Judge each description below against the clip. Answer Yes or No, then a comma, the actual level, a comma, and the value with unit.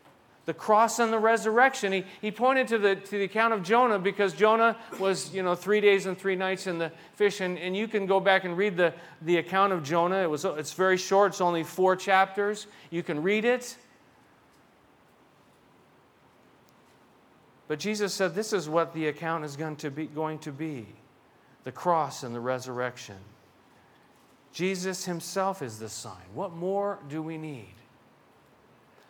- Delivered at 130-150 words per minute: No, average, 175 wpm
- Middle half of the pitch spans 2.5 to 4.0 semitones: No, average, 4.4 semitones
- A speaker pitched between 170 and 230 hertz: Yes, medium, 185 Hz